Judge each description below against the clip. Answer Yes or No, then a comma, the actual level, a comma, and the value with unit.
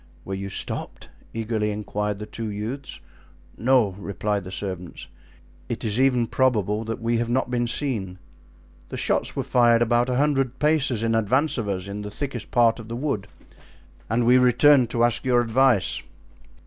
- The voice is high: No, low, 115 Hz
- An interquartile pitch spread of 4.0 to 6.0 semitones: No, average, 3.3 semitones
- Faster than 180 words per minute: No, average, 175 wpm